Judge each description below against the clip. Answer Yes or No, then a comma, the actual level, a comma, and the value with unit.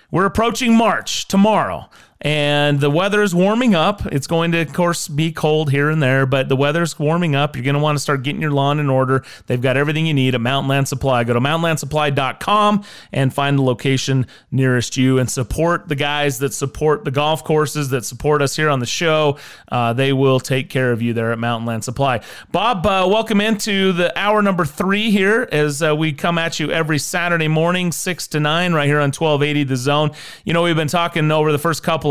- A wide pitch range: No, average, 3.8 semitones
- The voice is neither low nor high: Yes, medium, 150 Hz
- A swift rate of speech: Yes, fast, 220 wpm